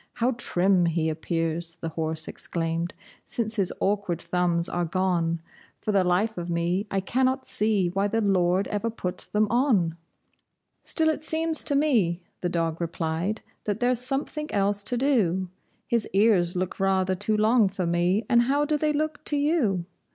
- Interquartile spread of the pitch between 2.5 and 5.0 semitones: No, wide, 5.5 semitones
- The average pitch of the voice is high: Yes, high, 195 Hz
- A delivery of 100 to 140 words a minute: No, average, 170 wpm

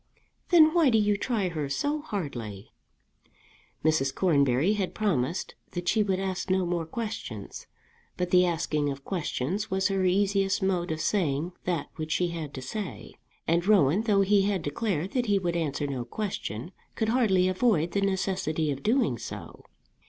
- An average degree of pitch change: Yes, average, 4.8 semitones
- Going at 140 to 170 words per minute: Yes, average, 165 wpm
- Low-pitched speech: No, medium, 185 Hz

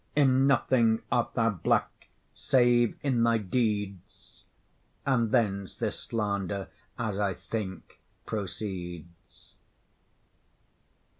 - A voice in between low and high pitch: No, low, 110 Hz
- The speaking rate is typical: No, slow, 90 wpm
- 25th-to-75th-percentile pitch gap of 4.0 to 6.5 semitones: No, average, 3.6 semitones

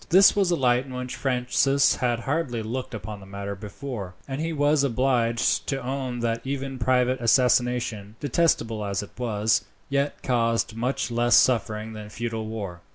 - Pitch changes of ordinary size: Yes, average, 3.2 semitones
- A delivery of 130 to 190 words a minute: Yes, average, 165 wpm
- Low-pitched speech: Yes, low, 120 Hz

